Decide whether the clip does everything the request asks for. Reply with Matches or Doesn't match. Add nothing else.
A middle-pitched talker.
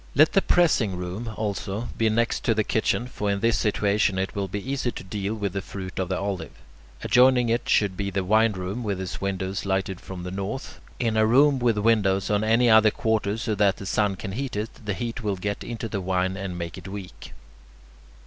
Doesn't match